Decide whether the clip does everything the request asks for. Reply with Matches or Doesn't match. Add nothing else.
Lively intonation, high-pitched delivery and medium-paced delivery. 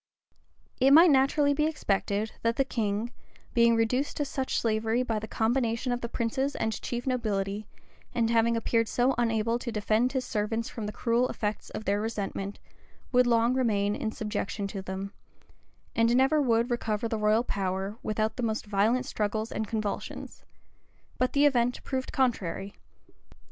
Doesn't match